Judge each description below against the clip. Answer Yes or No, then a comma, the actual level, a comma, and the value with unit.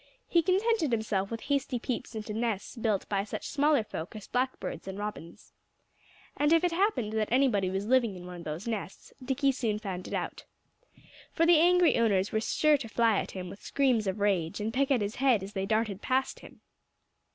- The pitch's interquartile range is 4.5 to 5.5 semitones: Yes, average, 5.2 semitones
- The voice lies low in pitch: No, high, 225 Hz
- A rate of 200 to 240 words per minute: Yes, fast, 205 wpm